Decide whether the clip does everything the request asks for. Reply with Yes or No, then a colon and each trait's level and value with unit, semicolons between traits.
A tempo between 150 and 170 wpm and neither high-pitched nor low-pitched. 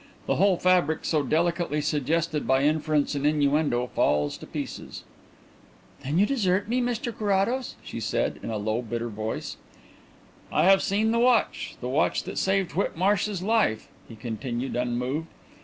Yes: average, 155 wpm; medium, 155 Hz